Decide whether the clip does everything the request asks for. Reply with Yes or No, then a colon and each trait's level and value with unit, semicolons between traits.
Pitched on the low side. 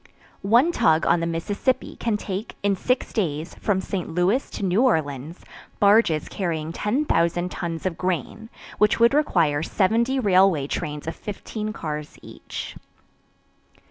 No: medium, 185 Hz